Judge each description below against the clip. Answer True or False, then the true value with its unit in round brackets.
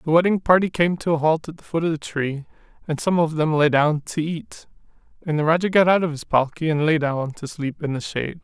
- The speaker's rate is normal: False (265 wpm)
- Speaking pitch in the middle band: True (160 Hz)